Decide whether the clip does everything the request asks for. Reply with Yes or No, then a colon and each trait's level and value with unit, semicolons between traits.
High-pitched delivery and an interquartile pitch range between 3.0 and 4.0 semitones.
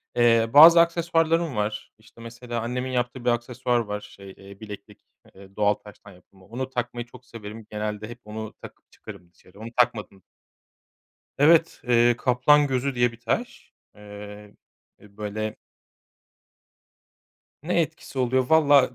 No: low, 120 Hz; average, 3.7 semitones